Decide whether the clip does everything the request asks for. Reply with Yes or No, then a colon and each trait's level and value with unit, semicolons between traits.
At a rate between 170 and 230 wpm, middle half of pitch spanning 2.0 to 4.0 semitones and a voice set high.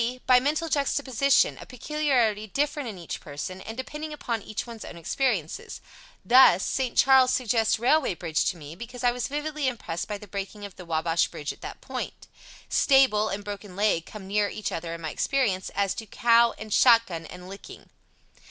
No: average, 190 wpm; wide, 5.6 semitones; high, 220 Hz